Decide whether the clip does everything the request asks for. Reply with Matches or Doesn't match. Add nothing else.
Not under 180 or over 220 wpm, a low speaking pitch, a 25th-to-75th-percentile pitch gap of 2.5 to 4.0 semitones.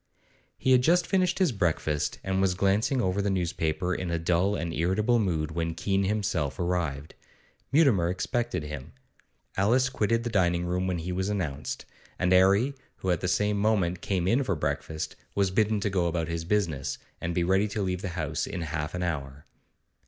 Matches